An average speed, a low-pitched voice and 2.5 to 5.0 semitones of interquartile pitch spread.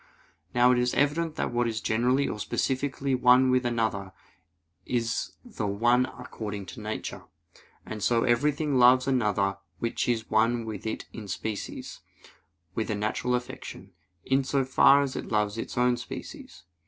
Yes: average, 155 wpm; low, 120 Hz; average, 2.9 semitones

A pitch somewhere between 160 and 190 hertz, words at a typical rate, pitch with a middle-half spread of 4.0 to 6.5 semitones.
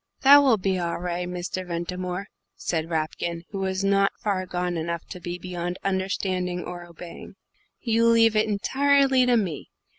No: medium, 185 Hz; average, 160 wpm; average, 3.2 semitones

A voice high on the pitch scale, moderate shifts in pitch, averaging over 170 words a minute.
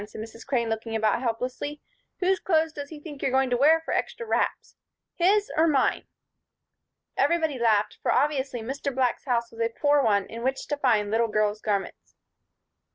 Yes: very high, 260 Hz; average, 4.6 semitones; average, 180 wpm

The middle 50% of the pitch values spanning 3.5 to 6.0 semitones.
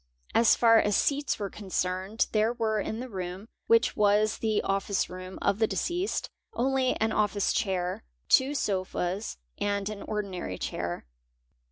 No: average, 3.1 semitones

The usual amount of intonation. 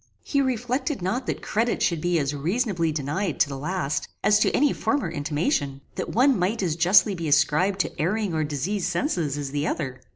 No: wide, 6.3 semitones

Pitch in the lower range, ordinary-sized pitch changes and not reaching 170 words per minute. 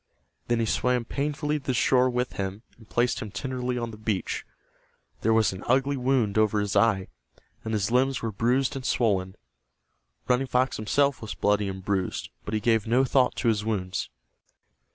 No: low, 115 Hz; average, 3.6 semitones; average, 185 wpm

